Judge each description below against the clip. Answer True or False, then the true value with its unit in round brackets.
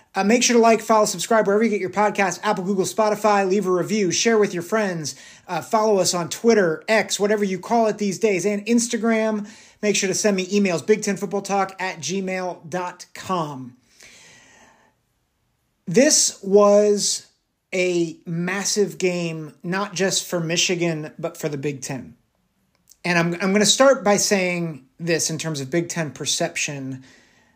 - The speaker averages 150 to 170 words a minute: True (165 wpm)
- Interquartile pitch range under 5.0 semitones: True (3.5 semitones)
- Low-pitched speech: False (190 Hz)